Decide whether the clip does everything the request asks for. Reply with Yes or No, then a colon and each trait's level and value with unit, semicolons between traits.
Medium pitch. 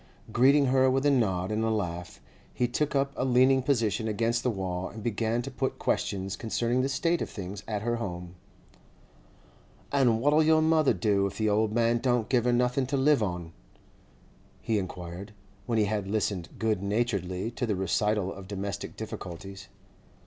No: low, 110 Hz